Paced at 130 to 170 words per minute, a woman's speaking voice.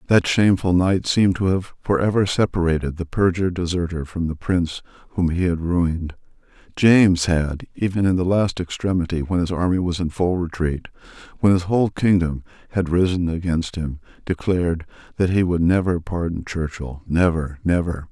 No: average, 165 wpm; male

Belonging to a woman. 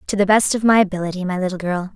Yes: female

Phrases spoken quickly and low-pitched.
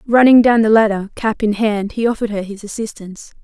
No: fast, 210 wpm; high, 215 Hz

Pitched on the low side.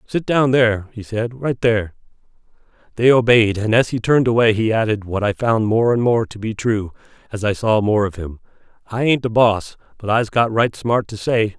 Yes: low, 110 Hz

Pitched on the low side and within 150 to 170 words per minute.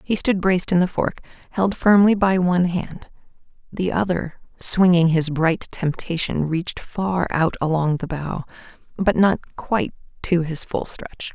No: medium, 175 Hz; average, 155 wpm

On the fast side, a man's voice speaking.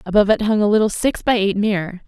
No: fast, 260 wpm; female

